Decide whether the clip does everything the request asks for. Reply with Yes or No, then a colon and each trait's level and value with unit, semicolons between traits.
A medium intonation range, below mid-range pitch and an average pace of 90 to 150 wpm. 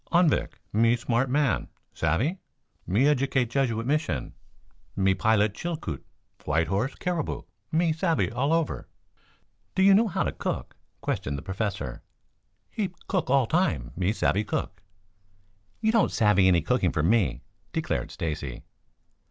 No: wide, 8.9 semitones; low, 115 Hz; slow, 135 wpm